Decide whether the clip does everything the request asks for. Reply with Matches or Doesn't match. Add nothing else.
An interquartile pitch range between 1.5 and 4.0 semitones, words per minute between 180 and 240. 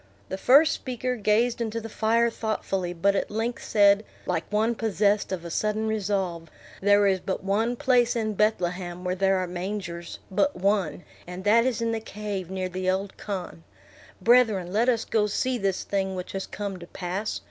Matches